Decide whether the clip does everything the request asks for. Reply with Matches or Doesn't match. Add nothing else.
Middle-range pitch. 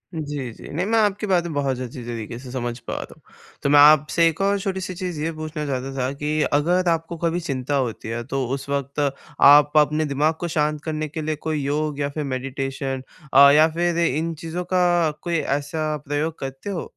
Matches